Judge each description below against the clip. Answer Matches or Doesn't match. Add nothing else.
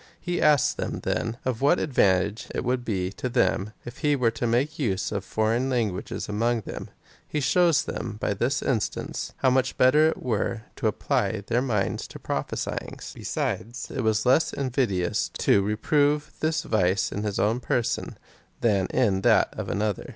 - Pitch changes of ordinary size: Matches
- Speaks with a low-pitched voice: Matches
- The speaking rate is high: Doesn't match